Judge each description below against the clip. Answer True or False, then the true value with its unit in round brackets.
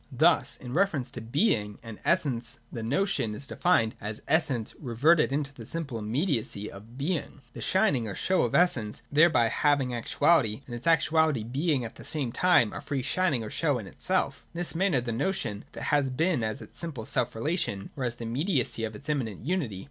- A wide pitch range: True (5.9 semitones)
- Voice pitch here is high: False (130 Hz)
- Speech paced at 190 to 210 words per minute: True (195 wpm)